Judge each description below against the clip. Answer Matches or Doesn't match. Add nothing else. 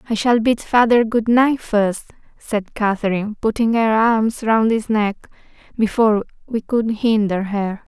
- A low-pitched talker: Doesn't match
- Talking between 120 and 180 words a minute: Matches